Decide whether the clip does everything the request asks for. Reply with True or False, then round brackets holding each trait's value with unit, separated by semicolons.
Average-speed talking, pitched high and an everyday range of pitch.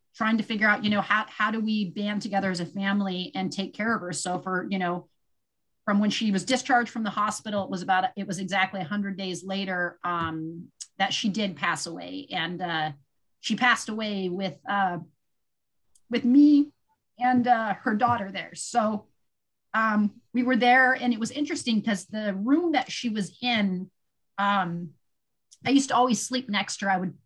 True (195 wpm; 205 Hz; 3.8 semitones)